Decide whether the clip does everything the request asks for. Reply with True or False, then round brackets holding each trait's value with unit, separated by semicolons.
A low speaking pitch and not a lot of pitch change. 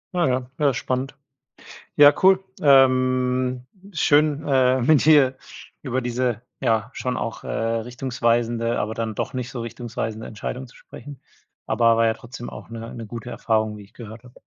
True (125 Hz; 2.3 semitones)